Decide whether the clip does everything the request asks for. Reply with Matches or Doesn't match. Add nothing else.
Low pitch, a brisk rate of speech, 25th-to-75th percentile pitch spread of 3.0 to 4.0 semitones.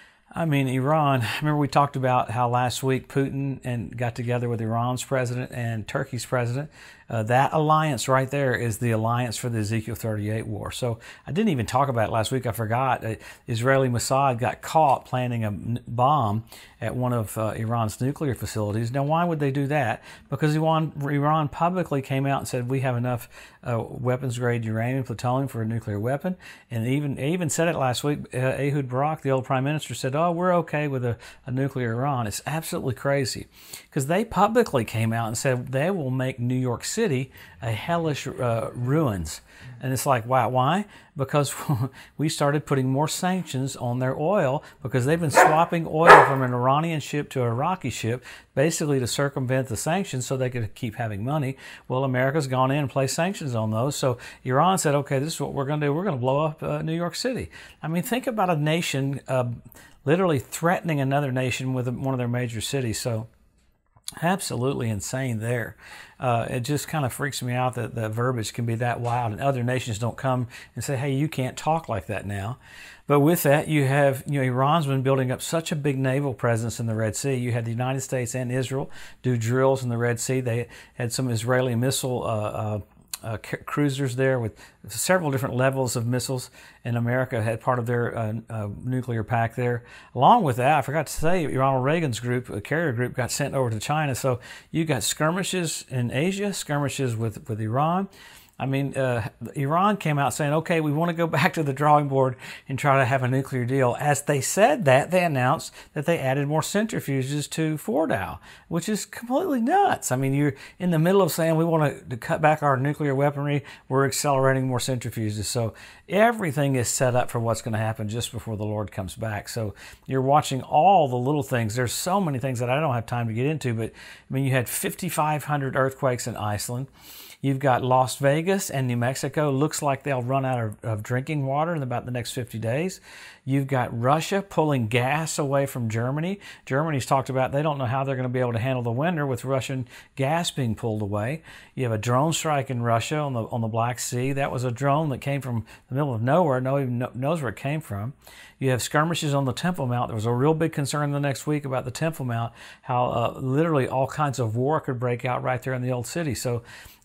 Matches